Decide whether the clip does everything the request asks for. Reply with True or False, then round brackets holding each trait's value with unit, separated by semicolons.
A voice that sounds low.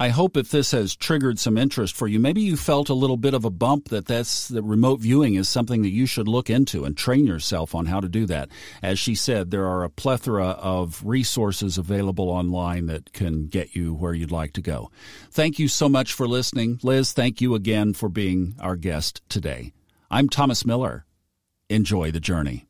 True (105 Hz)